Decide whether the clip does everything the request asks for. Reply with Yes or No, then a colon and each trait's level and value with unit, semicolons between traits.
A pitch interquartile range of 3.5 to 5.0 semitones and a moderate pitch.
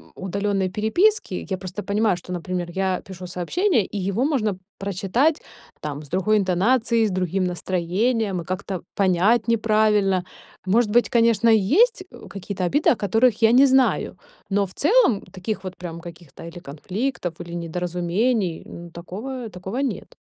No: average, 4.2 semitones; high, 195 Hz